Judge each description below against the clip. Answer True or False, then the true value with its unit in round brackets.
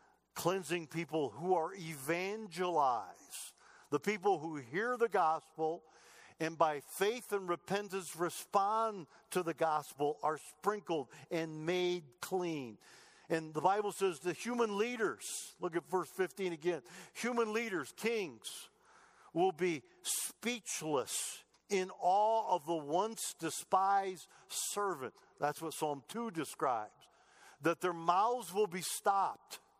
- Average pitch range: True (4.0 semitones)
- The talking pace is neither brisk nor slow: False (125 wpm)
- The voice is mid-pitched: True (180 Hz)